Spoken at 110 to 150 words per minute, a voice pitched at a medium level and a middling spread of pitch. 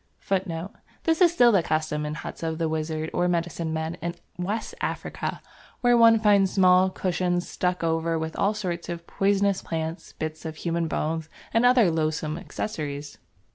No: average, 170 wpm; medium, 170 Hz; average, 3.6 semitones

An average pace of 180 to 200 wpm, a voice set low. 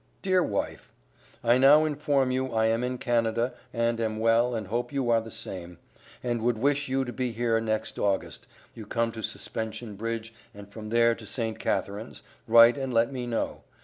Yes: average, 190 wpm; low, 115 Hz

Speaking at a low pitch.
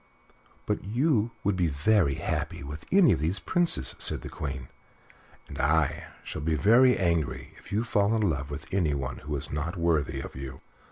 Yes: very low, 85 Hz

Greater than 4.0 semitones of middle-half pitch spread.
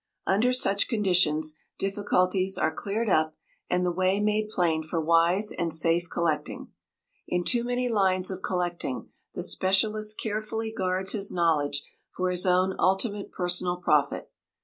No: average, 3.1 semitones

